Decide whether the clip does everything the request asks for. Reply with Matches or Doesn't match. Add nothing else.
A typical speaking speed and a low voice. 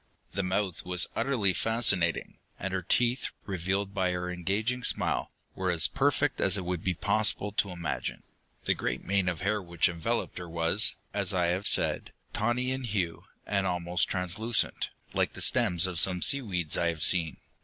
Matches